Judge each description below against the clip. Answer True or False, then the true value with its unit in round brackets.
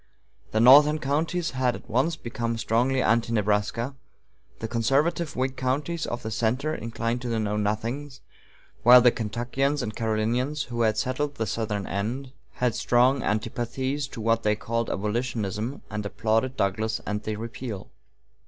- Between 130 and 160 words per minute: True (150 wpm)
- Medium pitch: False (120 Hz)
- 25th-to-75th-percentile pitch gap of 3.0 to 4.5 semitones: True (3.3 semitones)